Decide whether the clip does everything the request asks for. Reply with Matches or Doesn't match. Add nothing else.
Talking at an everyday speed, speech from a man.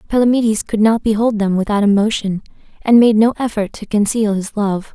Doesn't match